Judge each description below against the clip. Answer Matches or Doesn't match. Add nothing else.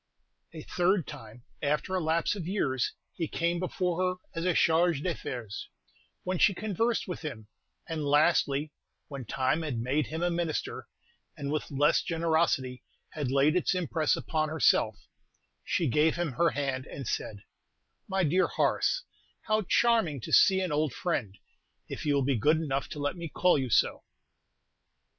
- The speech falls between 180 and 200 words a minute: Doesn't match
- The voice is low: Doesn't match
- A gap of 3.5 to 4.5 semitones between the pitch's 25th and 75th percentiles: Matches